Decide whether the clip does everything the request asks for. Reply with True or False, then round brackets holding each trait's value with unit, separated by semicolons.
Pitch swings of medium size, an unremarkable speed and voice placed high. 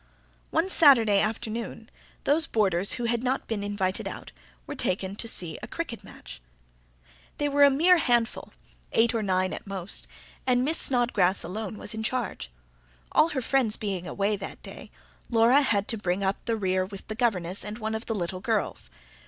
True (4.1 semitones; 185 wpm; 220 Hz)